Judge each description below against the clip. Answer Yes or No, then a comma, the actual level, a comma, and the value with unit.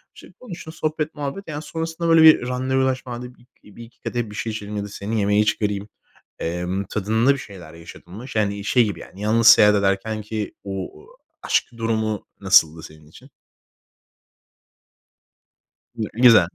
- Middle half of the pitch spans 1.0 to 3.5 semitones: No, average, 4.0 semitones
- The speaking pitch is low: Yes, low, 110 Hz